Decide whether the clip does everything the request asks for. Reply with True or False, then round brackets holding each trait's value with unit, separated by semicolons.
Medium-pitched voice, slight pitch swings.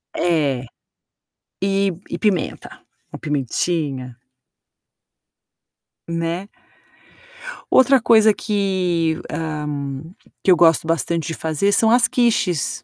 False (170 Hz; 4.2 semitones)